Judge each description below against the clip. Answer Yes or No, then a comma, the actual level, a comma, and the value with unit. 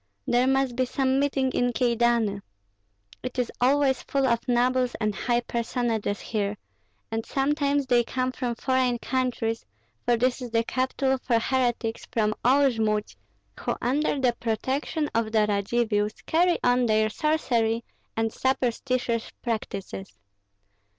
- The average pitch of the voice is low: No, high, 245 Hz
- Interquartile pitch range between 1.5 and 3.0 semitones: Yes, narrow, 2.6 semitones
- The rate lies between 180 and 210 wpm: No, slow, 135 wpm